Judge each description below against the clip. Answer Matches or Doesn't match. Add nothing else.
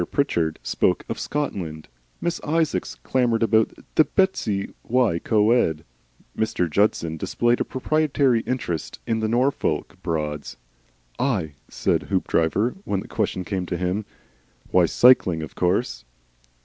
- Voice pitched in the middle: Doesn't match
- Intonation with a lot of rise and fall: Matches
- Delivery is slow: Matches